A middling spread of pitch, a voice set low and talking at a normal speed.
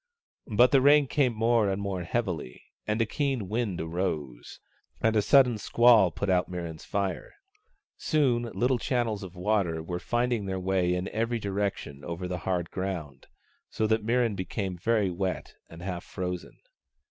Yes: average, 4.6 semitones; low, 100 Hz; average, 160 wpm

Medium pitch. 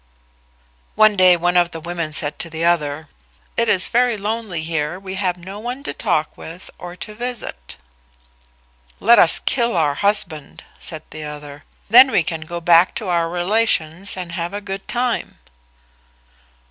Yes: medium, 175 Hz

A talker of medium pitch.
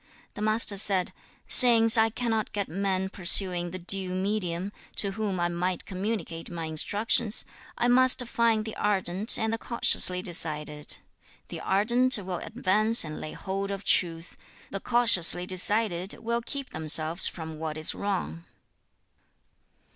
No: high, 195 Hz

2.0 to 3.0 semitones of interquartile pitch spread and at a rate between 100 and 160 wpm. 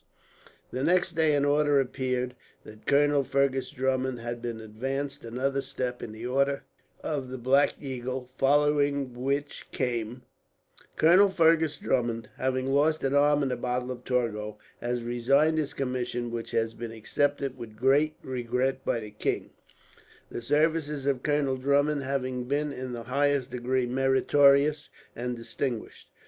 Yes: narrow, 2.6 semitones; average, 150 wpm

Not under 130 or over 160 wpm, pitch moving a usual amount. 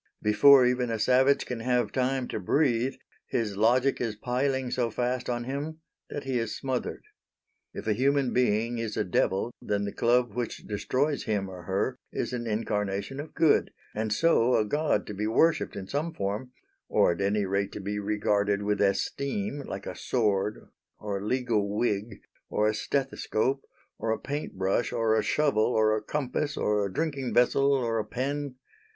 No: average, 180 wpm; average, 4.1 semitones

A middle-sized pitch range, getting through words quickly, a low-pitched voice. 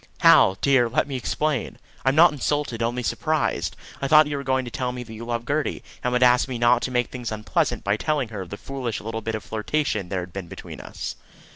Yes: average, 3.6 semitones; fast, 240 wpm; low, 125 Hz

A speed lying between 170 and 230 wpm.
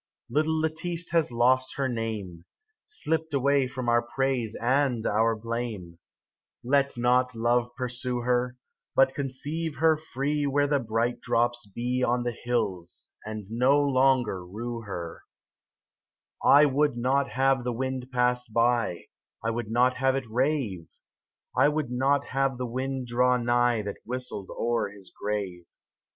No: average, 150 wpm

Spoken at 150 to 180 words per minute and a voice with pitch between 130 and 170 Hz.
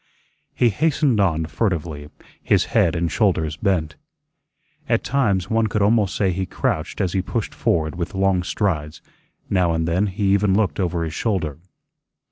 No: average, 160 wpm; very low, 95 Hz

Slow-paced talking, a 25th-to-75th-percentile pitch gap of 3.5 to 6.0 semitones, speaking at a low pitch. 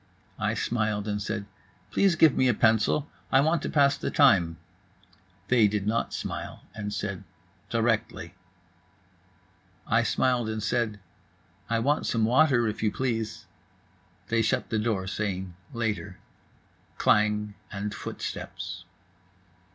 No: slow, 130 wpm; average, 2.7 semitones; low, 110 Hz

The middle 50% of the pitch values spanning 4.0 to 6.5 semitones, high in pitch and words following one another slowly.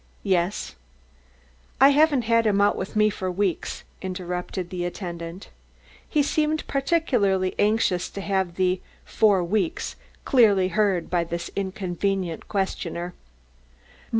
No: average, 3.3 semitones; high, 195 Hz; slow, 120 wpm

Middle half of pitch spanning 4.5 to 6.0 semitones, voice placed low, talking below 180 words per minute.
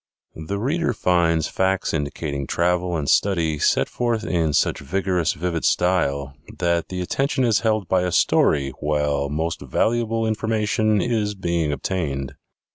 Yes: wide, 5.5 semitones; very low, 90 Hz; average, 140 wpm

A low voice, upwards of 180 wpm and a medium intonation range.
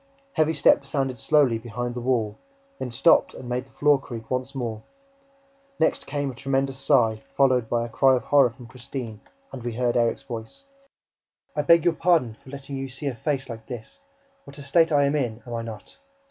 Yes: low, 130 Hz; average, 200 wpm; average, 3.0 semitones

